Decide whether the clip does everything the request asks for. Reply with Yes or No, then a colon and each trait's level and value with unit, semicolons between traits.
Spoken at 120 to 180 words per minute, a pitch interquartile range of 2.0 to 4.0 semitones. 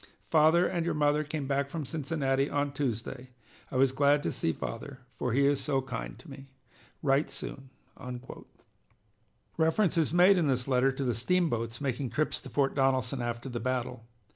Yes: average, 175 wpm; average, 2.9 semitones